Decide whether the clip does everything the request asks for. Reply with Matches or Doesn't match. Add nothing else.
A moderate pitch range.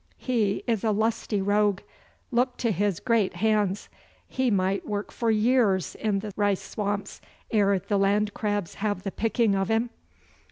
Doesn't match